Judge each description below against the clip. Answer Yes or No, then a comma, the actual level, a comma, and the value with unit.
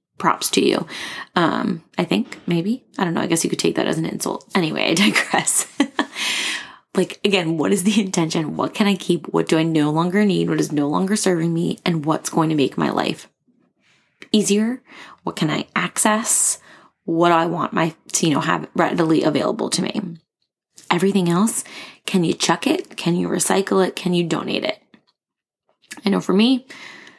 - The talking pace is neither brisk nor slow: Yes, average, 190 wpm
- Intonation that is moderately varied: Yes, average, 4.3 semitones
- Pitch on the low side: No, high, 190 Hz